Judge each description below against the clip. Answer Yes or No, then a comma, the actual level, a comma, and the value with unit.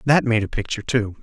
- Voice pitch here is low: Yes, low, 115 Hz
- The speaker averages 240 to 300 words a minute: Yes, fast, 245 wpm